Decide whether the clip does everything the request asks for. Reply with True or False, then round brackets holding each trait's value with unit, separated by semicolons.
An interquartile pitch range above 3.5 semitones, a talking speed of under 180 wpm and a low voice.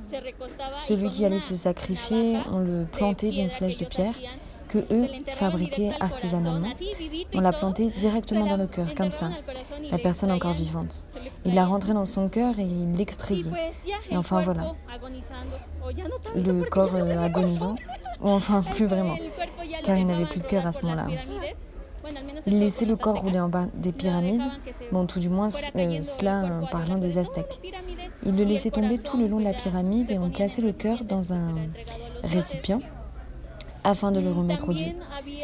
False (4.1 semitones; 170 wpm; 195 Hz)